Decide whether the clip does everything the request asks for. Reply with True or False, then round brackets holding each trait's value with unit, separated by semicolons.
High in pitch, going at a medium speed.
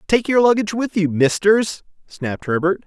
True (195 Hz; 165 wpm)